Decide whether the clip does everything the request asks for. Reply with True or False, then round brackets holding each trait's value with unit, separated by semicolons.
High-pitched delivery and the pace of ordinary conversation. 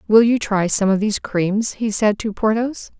False (210 Hz; 220 wpm)